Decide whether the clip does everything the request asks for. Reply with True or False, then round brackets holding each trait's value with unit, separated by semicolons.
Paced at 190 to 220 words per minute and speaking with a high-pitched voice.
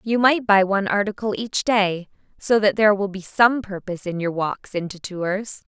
True (200 wpm; 200 Hz)